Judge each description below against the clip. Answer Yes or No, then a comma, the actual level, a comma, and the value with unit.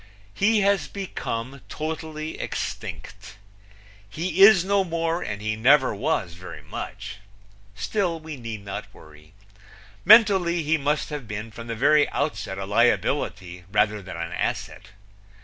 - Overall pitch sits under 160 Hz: Yes, medium, 140 Hz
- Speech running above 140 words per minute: No, slow, 135 wpm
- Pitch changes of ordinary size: No, wide, 8.1 semitones